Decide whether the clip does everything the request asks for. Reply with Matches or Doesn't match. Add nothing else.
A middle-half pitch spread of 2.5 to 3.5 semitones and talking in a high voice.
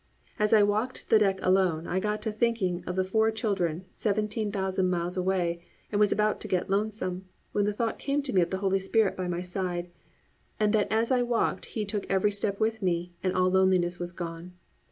Matches